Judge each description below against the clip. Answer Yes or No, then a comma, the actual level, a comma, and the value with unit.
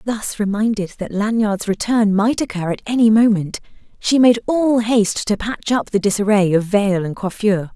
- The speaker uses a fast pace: No, average, 180 wpm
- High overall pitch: Yes, high, 210 Hz